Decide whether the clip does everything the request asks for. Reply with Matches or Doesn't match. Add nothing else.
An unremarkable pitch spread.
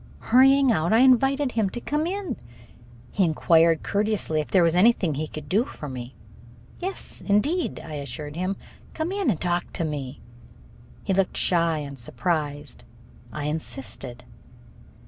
Doesn't match